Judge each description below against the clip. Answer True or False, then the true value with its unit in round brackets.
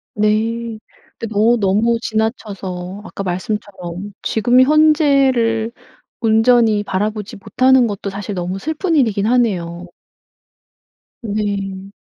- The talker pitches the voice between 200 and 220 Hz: True (215 Hz)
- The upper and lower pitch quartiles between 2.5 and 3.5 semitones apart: True (3.1 semitones)